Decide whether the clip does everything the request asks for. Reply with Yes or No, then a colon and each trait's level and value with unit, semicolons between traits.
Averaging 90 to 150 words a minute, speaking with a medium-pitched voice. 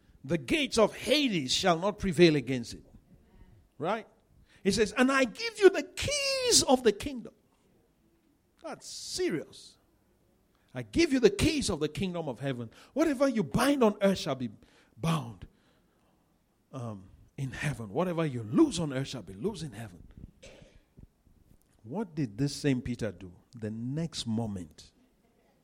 Yes: average, 145 wpm; medium, 155 Hz